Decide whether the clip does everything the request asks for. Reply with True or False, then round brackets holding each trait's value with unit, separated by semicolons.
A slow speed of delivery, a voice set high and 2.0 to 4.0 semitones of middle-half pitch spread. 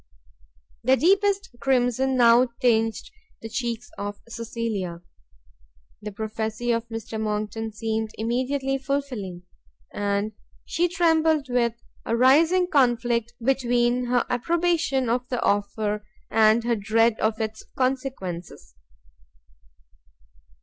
True (105 wpm; 235 Hz; 3.3 semitones)